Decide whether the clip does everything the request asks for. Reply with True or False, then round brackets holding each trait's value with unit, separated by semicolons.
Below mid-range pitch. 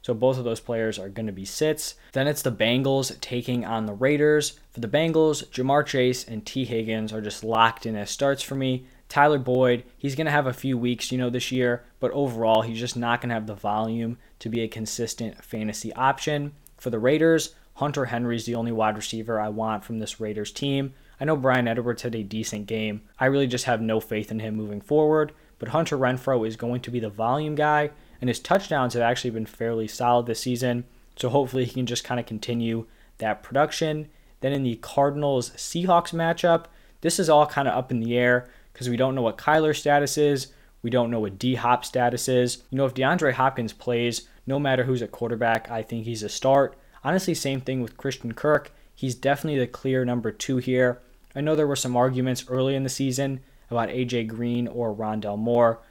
True (125 Hz)